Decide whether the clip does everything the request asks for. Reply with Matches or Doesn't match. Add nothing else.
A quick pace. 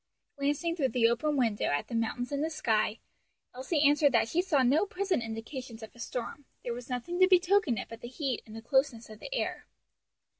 Matches